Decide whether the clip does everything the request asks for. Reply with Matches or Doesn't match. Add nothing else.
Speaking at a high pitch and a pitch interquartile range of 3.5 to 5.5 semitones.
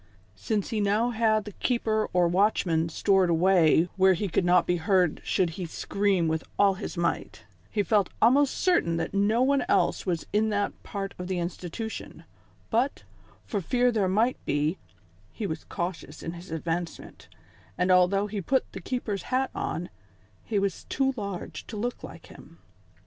Matches